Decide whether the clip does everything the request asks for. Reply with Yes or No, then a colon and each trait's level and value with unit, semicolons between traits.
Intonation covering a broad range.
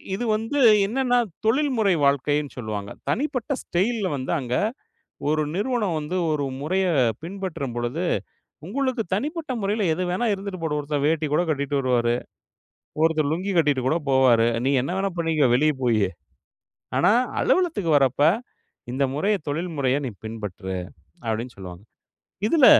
Yes: wide, 7.4 semitones